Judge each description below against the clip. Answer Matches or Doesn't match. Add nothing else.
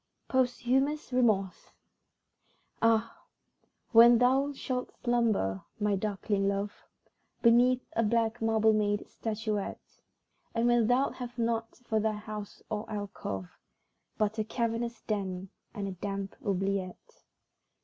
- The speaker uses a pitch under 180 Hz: Doesn't match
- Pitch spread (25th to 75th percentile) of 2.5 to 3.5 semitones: Matches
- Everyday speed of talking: Doesn't match